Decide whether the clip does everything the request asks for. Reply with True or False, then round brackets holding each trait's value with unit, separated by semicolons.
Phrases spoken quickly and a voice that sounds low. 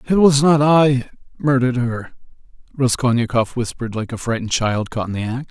False (175 wpm; 125 Hz)